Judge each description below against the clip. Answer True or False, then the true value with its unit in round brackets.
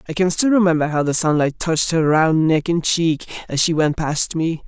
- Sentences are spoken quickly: True (230 wpm)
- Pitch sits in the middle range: True (160 Hz)